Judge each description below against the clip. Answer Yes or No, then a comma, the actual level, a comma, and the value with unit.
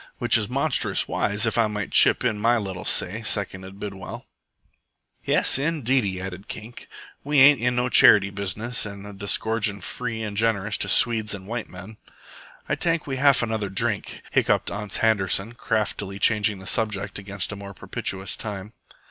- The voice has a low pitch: Yes, low, 105 Hz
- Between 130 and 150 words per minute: No, average, 165 wpm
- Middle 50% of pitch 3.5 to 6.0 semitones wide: No, average, 2.7 semitones